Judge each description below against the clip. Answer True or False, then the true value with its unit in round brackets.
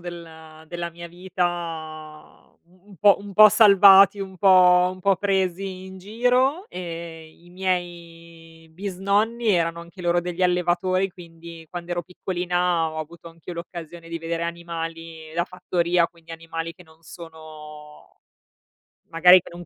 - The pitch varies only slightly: True (1.9 semitones)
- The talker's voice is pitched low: False (175 Hz)